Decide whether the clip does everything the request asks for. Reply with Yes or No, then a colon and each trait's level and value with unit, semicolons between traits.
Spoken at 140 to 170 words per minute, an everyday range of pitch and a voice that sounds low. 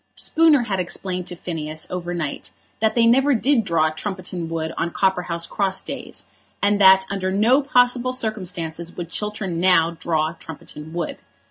No: average, 155 wpm; average, 4.5 semitones; medium, 185 Hz